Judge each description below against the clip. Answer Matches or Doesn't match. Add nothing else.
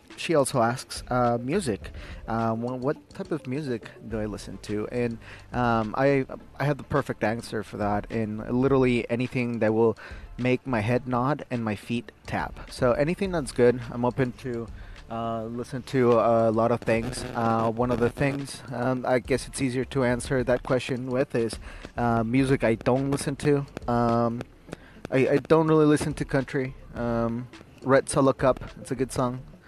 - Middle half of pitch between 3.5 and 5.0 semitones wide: Doesn't match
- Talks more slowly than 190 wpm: Matches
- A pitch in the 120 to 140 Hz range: Matches